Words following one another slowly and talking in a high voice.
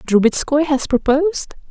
Yes: slow, 105 wpm; very high, 280 Hz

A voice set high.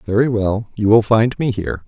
No: low, 110 Hz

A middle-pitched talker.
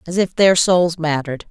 Yes: medium, 170 Hz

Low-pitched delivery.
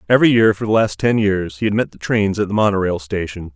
Yes: low, 100 Hz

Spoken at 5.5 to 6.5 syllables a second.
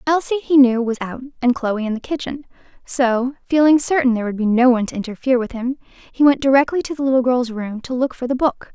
Yes: 6.2 syllables/s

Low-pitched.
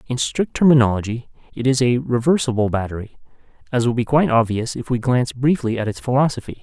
Yes: low, 125 Hz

